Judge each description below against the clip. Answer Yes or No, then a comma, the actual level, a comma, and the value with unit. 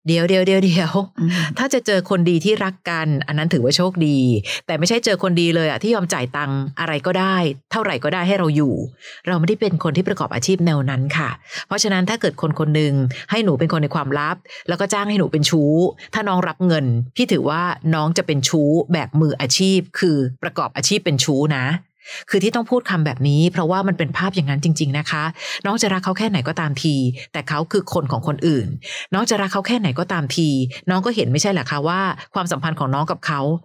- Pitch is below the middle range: No, medium, 165 Hz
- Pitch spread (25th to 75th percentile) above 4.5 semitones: No, average, 4.2 semitones